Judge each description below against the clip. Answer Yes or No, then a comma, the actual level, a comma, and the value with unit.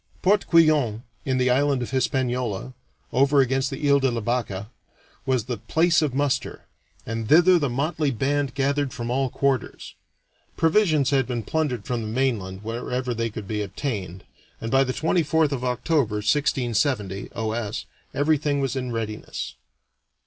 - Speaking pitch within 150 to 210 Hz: No, low, 130 Hz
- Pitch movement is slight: No, average, 3.7 semitones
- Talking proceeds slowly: No, average, 155 wpm